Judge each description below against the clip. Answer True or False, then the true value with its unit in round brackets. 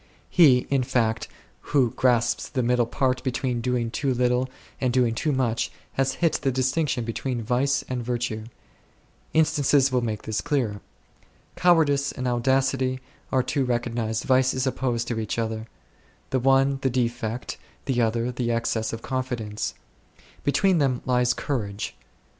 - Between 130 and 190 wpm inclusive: True (145 wpm)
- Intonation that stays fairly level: True (2.3 semitones)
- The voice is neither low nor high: False (125 Hz)